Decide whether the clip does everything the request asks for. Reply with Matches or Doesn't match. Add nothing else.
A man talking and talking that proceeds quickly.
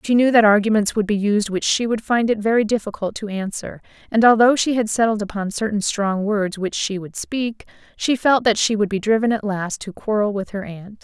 Doesn't match